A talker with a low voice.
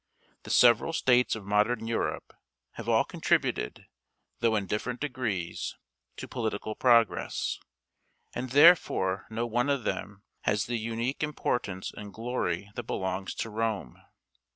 Yes: low, 115 Hz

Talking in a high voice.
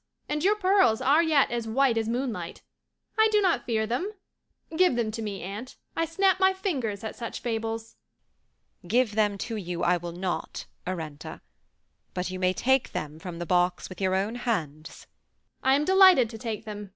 Yes: high, 225 Hz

